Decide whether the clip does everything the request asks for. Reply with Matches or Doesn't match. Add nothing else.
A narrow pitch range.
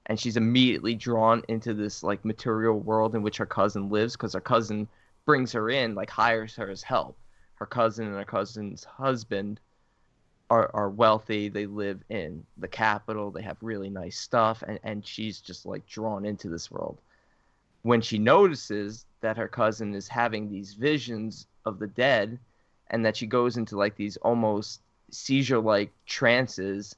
Matches